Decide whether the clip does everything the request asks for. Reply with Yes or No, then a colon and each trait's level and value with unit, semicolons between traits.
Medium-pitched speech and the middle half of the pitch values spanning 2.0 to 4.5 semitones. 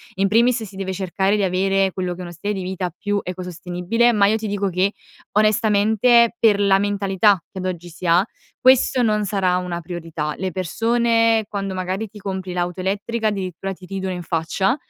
No: high, 195 Hz; narrow, 2.6 semitones